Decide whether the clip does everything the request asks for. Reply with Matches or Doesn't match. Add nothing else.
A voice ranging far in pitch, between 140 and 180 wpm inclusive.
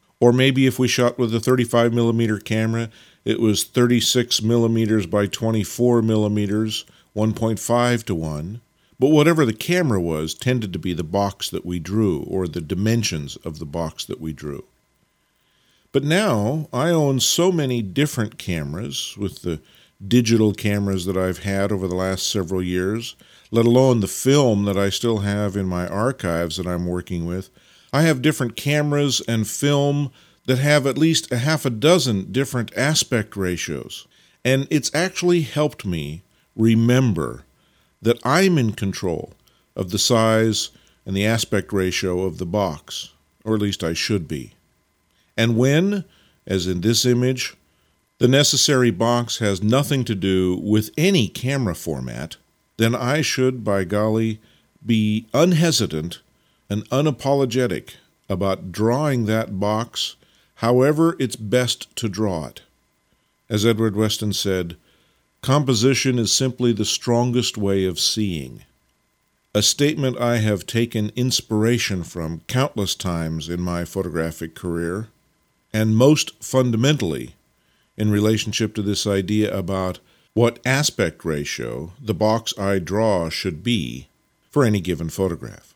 Doesn't match